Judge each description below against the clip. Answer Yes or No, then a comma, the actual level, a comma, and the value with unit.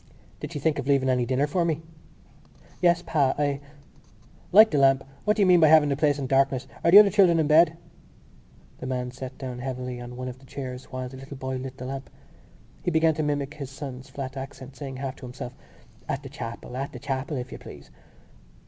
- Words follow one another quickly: Yes, fast, 220 wpm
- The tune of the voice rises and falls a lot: No, narrow, 2.6 semitones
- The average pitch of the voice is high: No, low, 135 Hz